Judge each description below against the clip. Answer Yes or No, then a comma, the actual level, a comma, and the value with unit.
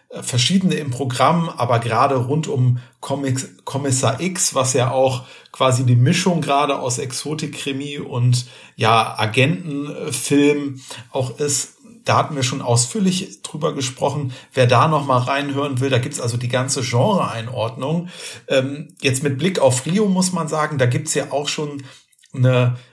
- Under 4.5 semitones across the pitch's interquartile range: Yes, average, 2.8 semitones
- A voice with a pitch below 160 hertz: Yes, low, 135 Hz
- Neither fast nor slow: Yes, average, 150 wpm